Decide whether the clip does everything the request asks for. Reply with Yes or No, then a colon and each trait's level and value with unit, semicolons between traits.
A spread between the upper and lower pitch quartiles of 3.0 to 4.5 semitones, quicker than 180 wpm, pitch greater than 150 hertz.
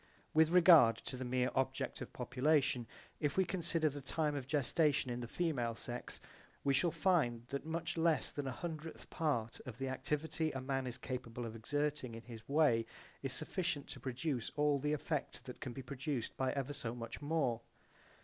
No: average, 3.9 semitones; average, 190 wpm; medium, 140 Hz